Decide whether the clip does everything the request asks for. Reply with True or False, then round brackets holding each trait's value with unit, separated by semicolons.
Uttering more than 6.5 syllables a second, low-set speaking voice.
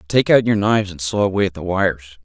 True (6.9 syllables/s; 95 Hz)